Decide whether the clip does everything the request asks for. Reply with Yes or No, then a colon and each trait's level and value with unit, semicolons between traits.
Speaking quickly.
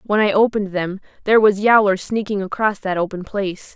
No: average, 190 wpm